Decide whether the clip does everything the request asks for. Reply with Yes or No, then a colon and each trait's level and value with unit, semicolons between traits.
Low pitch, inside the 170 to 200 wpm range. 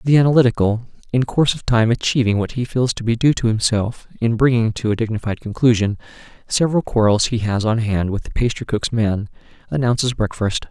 Yes: low, 115 Hz; average, 185 wpm